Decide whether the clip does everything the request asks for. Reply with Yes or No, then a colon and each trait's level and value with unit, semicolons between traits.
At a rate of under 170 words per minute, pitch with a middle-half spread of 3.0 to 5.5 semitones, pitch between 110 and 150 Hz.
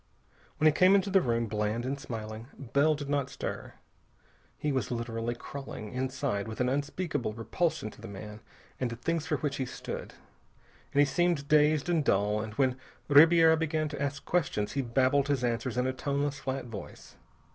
No: average, 185 wpm; average, 4.4 semitones; low, 135 Hz